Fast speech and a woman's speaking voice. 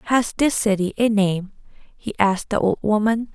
No: average, 180 wpm; female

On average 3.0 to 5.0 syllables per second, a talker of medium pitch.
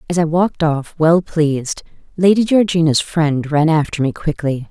Yes: 4.8 syllables/s; medium, 160 Hz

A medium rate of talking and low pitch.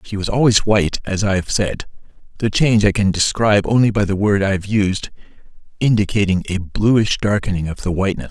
Yes: average, 195 wpm; low, 100 Hz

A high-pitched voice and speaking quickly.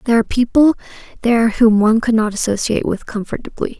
No: high, 225 Hz; average, 175 wpm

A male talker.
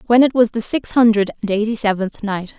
No: female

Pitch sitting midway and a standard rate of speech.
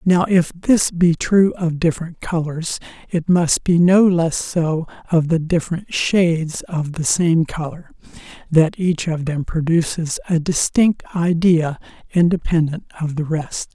Yes: medium, 165 Hz; average, 150 wpm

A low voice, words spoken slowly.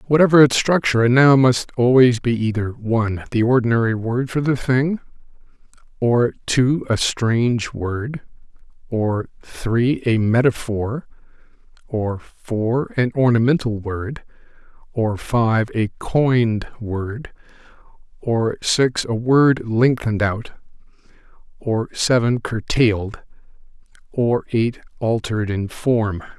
Yes: low, 120 Hz; slow, 110 wpm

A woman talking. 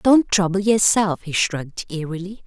Yes: female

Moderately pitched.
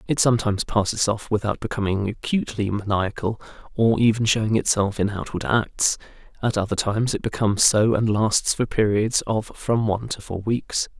No: low, 110 Hz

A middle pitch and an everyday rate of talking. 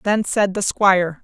No: high, 195 Hz; average, 195 wpm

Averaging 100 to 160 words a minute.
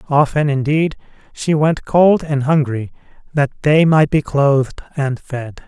Yes: average, 150 wpm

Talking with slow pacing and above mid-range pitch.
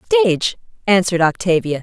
Yes: slow, 100 wpm; high, 195 Hz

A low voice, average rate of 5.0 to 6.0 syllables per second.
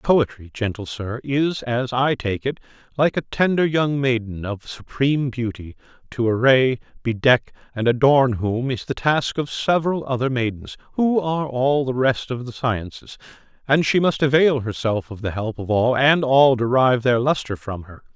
No: low, 125 Hz; 4.7 syllables/s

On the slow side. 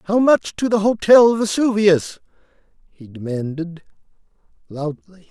Yes: slow, 100 wpm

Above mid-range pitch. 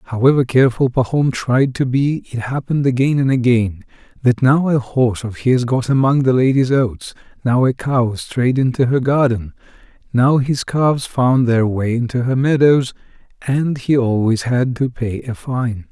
No: low, 125 Hz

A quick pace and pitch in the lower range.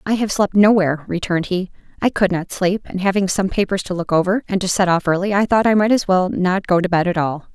No: fast, 270 wpm; high, 190 Hz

